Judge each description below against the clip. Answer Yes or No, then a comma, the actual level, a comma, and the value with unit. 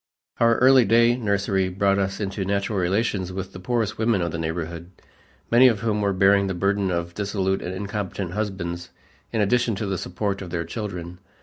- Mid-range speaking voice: No, low, 100 Hz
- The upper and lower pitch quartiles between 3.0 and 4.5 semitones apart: No, narrow, 2.6 semitones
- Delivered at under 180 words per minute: No, average, 190 wpm